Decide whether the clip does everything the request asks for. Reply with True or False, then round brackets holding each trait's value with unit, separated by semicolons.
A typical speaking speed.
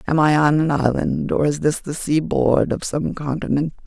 False (220 wpm)